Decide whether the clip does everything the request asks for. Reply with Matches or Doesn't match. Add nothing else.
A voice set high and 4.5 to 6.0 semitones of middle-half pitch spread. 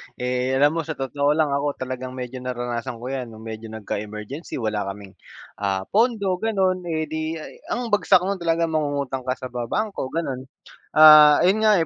Doesn't match